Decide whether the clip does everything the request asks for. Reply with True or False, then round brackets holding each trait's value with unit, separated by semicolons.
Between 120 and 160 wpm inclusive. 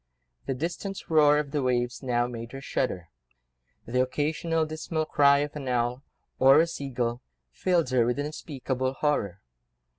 True (155 wpm)